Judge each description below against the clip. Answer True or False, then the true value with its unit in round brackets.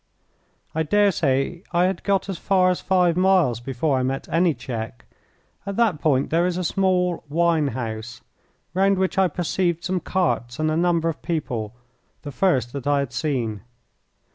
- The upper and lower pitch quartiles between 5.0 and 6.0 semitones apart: True (5.6 semitones)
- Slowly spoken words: False (175 wpm)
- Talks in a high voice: False (165 Hz)